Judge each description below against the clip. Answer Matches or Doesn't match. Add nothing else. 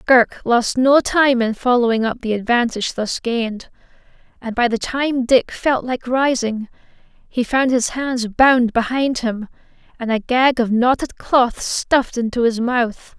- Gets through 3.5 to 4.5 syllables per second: Matches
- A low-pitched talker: Doesn't match